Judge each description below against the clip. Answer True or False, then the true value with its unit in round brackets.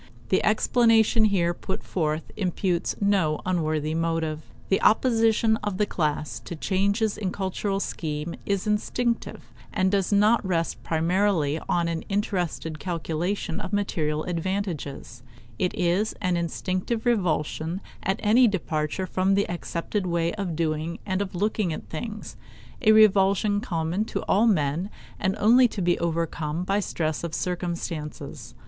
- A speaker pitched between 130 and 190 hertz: True (185 Hz)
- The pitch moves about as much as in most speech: True (3.8 semitones)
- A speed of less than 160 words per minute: True (140 wpm)